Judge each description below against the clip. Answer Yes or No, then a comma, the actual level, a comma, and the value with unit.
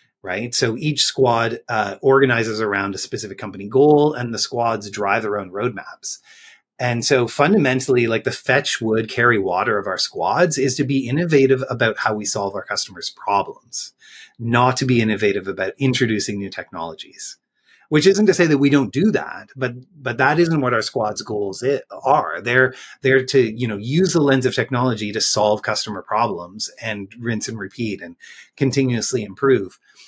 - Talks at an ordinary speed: Yes, average, 180 wpm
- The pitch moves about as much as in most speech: Yes, average, 3.8 semitones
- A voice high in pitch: No, low, 120 Hz